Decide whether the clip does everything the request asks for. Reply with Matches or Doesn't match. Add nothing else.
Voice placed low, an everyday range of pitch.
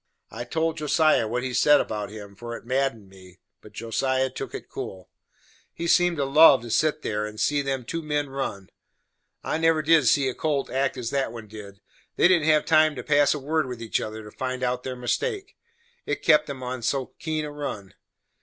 Matches